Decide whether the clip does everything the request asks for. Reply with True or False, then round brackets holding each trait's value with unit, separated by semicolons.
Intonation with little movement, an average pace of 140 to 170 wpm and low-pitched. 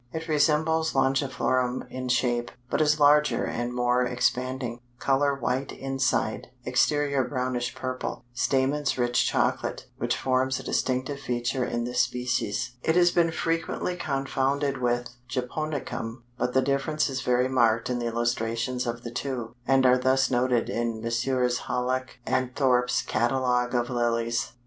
True (1.9 semitones; 145 wpm; 125 Hz)